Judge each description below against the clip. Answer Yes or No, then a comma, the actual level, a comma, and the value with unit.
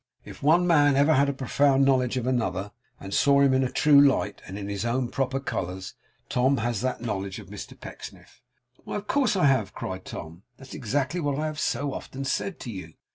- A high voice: No, low, 130 Hz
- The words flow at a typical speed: No, fast, 215 wpm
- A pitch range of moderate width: Yes, average, 4.2 semitones